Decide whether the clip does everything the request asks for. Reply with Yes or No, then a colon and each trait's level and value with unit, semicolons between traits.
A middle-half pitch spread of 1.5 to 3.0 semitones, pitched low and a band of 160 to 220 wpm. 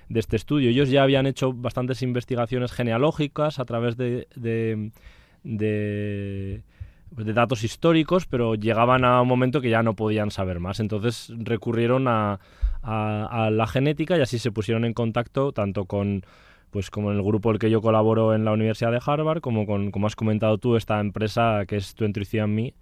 Yes: narrow, 2.6 semitones; low, 115 Hz; average, 185 wpm